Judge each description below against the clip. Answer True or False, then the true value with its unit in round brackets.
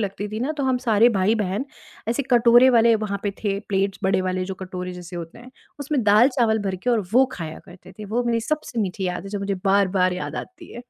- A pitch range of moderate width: True (4.0 semitones)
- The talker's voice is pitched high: True (205 Hz)